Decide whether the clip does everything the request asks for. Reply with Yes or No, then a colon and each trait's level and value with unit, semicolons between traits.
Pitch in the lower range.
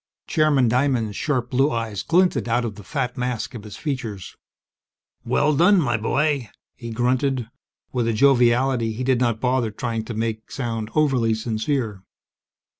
Yes: low, 120 Hz